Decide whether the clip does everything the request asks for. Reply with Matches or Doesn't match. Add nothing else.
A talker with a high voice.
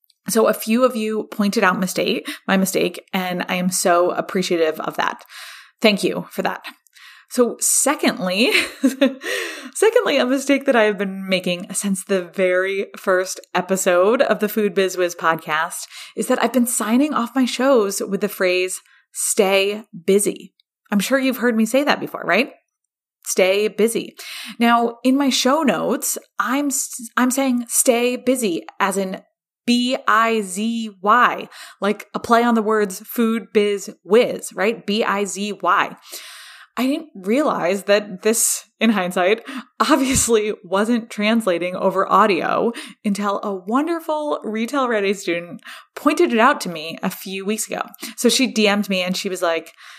Matches